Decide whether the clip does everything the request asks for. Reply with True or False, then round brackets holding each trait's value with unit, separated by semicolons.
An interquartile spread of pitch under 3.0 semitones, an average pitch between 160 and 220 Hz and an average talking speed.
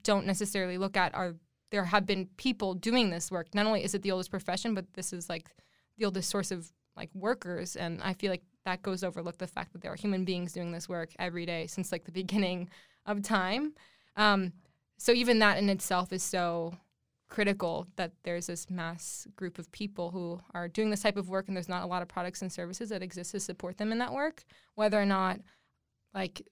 False (2.6 semitones; 185 Hz; 220 wpm)